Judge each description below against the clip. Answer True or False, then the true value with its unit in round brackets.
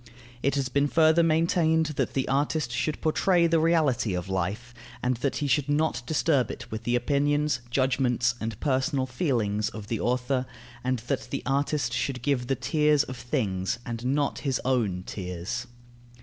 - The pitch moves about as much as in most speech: True (3.6 semitones)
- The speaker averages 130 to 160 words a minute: False (170 wpm)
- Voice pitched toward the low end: True (130 Hz)